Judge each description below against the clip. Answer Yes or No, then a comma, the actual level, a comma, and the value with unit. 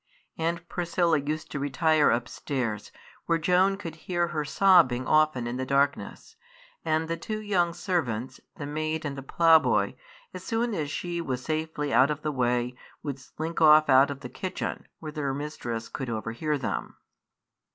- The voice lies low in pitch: No, medium, 155 Hz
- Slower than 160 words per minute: No, average, 165 wpm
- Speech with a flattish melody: No, average, 3.9 semitones